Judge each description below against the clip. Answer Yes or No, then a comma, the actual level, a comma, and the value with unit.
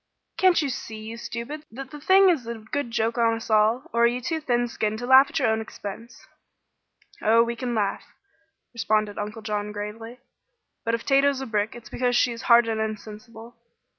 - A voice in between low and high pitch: No, high, 230 Hz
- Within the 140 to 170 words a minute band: No, average, 200 wpm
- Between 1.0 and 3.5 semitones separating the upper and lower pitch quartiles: Yes, narrow, 2.5 semitones